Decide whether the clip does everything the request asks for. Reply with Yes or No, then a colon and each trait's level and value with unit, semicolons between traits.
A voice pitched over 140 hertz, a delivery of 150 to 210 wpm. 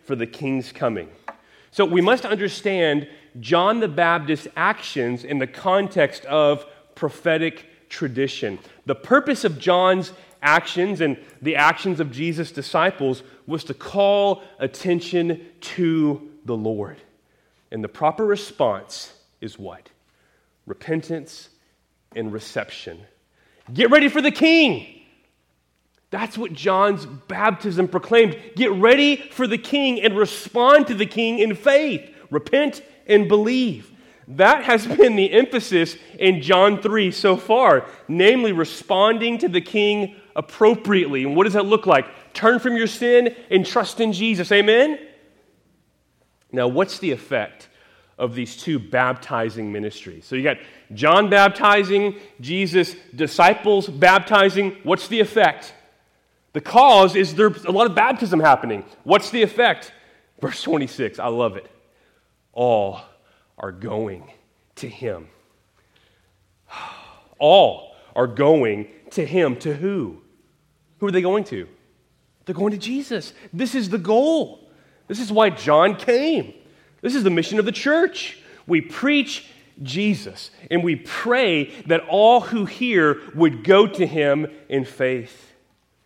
No: medium, 185 Hz; slow, 135 wpm